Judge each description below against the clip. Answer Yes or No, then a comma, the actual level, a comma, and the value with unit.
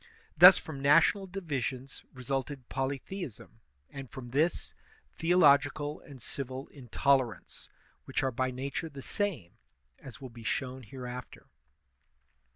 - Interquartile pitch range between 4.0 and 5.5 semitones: No, narrow, 2.6 semitones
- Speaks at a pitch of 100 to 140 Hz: Yes, low, 135 Hz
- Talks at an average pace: No, slow, 115 wpm